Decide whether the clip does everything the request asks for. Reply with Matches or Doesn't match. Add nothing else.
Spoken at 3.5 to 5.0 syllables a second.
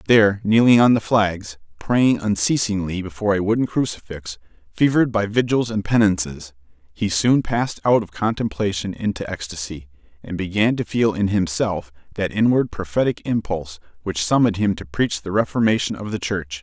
Doesn't match